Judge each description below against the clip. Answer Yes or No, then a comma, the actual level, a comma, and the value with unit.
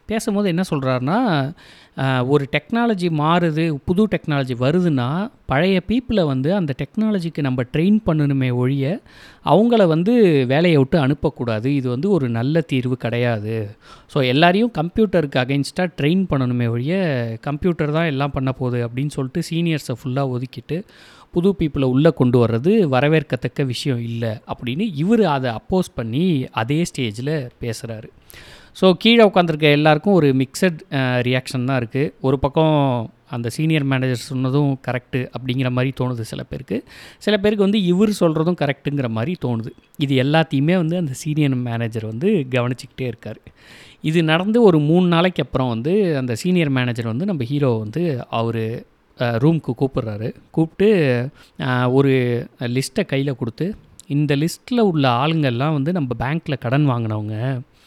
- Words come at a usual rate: No, fast, 135 wpm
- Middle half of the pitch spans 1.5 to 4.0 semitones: No, average, 5.2 semitones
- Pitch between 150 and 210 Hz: No, medium, 140 Hz